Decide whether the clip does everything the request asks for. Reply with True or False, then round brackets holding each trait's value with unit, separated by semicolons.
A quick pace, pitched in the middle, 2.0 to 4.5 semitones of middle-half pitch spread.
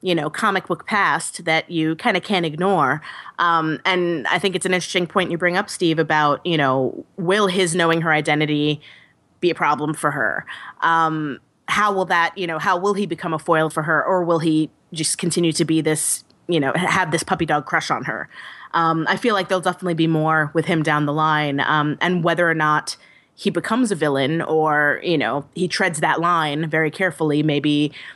True (210 wpm; 165 Hz; 2.8 semitones)